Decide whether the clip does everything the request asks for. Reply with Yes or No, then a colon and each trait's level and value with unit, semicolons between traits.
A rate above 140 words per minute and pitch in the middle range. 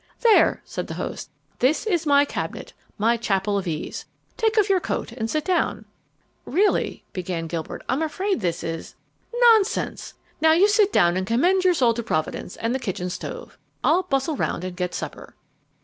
No: average, 180 wpm; very high, 260 Hz